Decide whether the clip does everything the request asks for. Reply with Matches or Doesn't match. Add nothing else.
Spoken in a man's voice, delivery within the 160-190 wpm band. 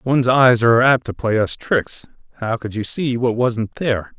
Doesn't match